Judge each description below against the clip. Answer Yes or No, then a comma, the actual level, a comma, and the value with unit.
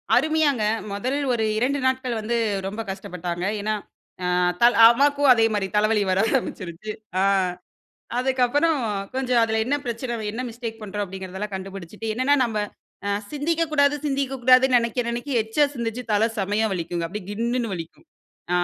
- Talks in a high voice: Yes, high, 230 Hz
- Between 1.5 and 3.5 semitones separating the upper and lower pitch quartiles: No, average, 4.1 semitones